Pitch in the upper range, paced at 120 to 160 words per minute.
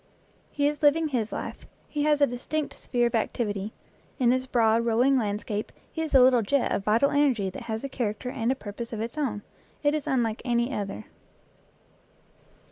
No: high, 240 Hz; average, 190 wpm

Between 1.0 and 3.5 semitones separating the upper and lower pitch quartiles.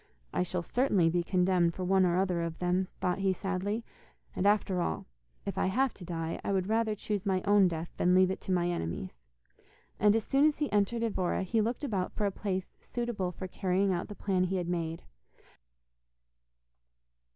Yes: narrow, 2.6 semitones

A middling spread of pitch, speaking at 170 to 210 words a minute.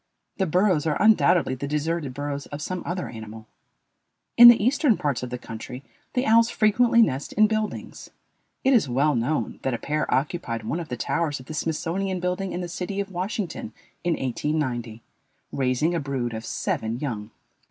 No: wide, 6.7 semitones; average, 180 wpm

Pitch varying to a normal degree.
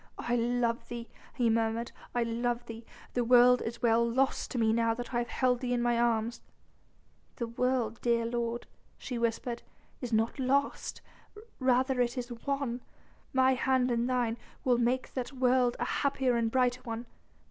No: narrow, 1.4 semitones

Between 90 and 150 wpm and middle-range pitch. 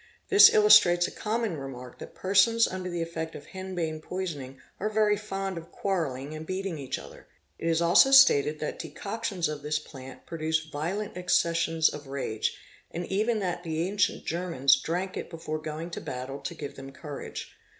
No: average, 175 wpm; medium, 170 Hz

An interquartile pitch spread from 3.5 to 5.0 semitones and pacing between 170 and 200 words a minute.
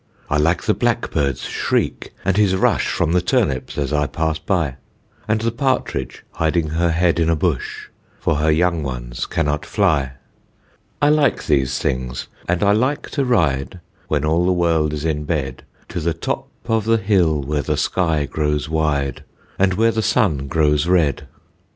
Yes: average, 4.1 semitones; average, 175 wpm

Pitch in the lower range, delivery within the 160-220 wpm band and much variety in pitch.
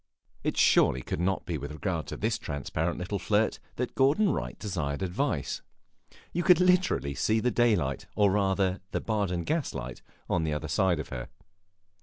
Yes: very low, 95 Hz; average, 170 wpm; wide, 6.7 semitones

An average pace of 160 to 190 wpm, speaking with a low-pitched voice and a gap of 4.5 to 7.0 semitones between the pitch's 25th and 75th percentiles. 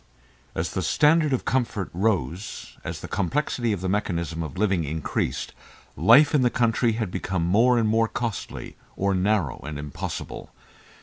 Yes: average, 165 wpm; low, 100 Hz; wide, 5.6 semitones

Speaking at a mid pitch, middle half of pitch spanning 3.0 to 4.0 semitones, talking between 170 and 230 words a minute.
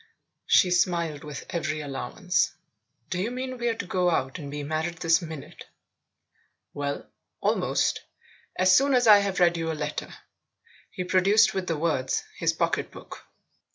No: medium, 175 Hz; average, 3.7 semitones; average, 160 wpm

